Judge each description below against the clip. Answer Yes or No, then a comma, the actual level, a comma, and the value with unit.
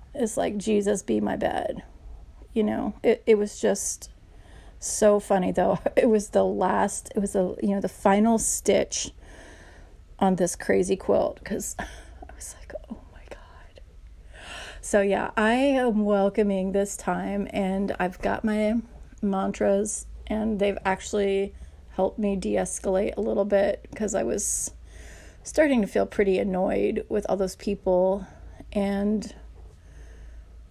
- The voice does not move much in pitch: Yes, narrow, 2.0 semitones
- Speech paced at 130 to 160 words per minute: Yes, average, 140 wpm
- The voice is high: Yes, high, 200 Hz